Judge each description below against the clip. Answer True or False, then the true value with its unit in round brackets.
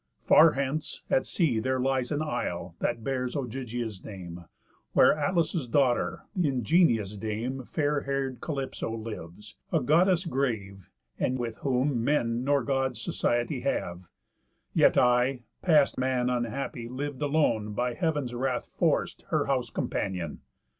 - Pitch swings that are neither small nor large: True (3.6 semitones)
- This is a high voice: False (125 Hz)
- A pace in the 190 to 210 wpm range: False (135 wpm)